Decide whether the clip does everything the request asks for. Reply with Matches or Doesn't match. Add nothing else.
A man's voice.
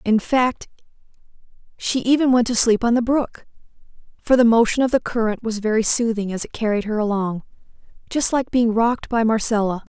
Doesn't match